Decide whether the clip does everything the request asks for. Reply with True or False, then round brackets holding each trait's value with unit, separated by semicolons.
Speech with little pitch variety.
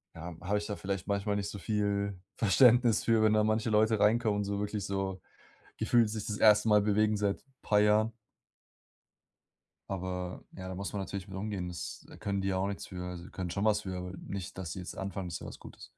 True (2.0 semitones)